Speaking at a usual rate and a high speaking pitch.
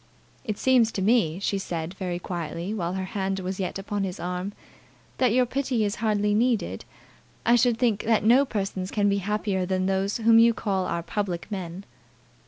Yes: average, 190 wpm; high, 200 Hz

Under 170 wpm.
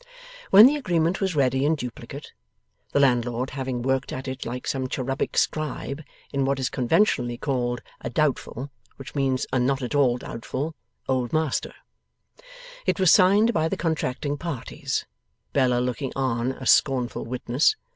Yes: average, 155 wpm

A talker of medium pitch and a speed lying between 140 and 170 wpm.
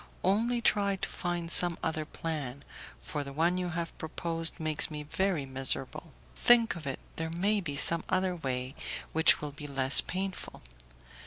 Yes: medium, 165 Hz; average, 165 wpm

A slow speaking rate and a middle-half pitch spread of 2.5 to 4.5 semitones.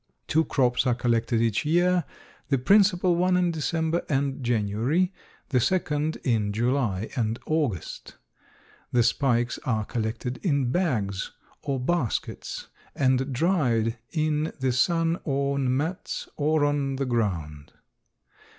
No: slow, 125 wpm; average, 5.2 semitones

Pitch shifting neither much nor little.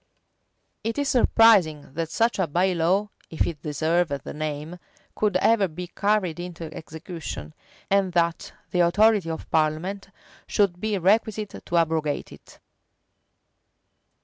Yes: average, 4.0 semitones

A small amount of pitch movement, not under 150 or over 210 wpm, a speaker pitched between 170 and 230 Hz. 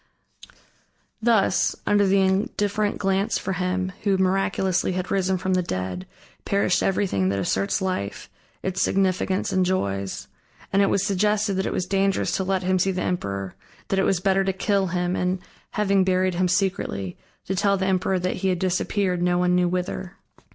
Yes: narrow, 1.3 semitones; average, 180 wpm; medium, 185 Hz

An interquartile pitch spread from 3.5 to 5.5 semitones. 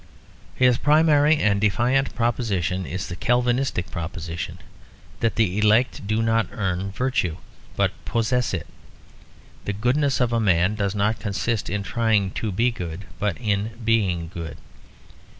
Yes: average, 4.1 semitones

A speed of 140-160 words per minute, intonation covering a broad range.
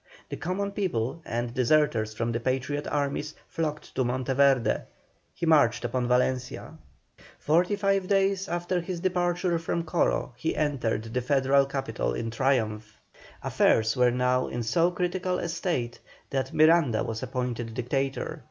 Yes: average, 145 wpm; wide, 5.9 semitones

